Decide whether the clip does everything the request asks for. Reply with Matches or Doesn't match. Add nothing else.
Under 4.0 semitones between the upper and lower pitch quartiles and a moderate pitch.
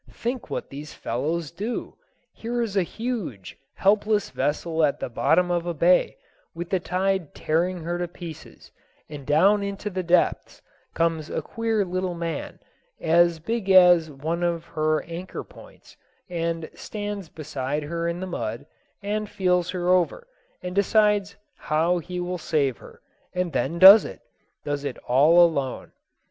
Matches